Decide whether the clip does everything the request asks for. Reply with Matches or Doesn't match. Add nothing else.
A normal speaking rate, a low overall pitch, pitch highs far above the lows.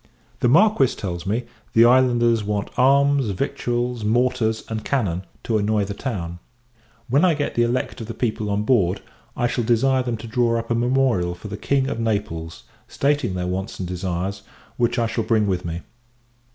Doesn't match